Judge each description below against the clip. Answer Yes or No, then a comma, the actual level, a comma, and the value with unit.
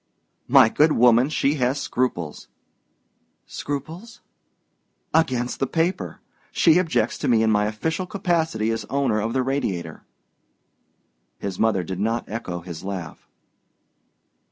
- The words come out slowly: Yes, slow, 125 wpm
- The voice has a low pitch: Yes, low, 120 Hz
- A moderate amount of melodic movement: No, wide, 6.8 semitones